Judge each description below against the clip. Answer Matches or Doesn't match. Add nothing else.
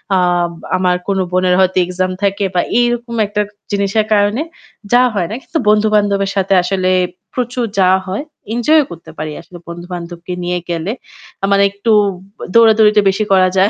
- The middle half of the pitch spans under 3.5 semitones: Matches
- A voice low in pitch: Doesn't match